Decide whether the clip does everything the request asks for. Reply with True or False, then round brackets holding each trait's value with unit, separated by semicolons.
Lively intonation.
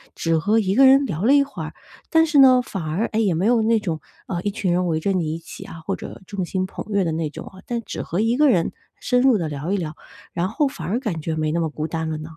True (5.7 semitones)